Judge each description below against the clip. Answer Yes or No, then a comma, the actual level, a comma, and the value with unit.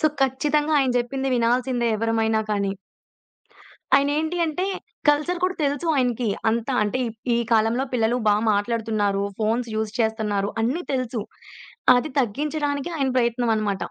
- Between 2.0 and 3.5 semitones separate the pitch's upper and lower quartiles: No, average, 4.2 semitones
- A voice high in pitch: Yes, high, 240 Hz